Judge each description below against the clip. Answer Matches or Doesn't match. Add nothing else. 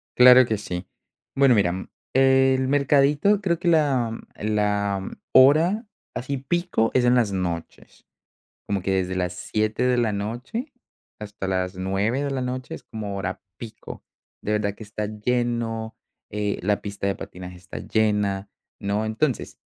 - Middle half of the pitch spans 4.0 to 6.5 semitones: Matches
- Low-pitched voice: Matches